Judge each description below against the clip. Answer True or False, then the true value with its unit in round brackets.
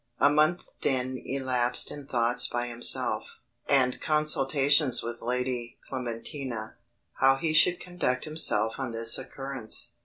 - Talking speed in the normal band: False (125 wpm)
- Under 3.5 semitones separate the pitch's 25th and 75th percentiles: True (3.0 semitones)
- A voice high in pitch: False (130 Hz)